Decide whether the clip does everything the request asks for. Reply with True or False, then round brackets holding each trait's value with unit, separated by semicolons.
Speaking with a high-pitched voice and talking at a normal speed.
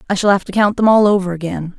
False (195 Hz; 300 wpm)